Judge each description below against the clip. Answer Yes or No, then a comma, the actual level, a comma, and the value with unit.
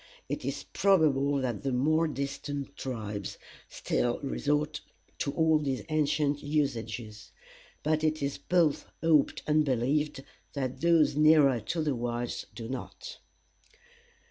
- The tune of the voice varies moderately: Yes, average, 3.2 semitones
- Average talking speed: No, slow, 125 wpm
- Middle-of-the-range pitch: Yes, medium, 145 Hz